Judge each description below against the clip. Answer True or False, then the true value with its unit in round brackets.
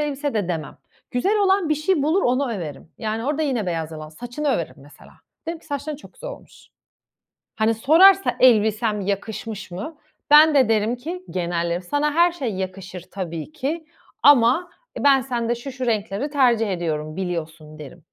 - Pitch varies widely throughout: True (8.1 semitones)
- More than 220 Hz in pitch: True (235 Hz)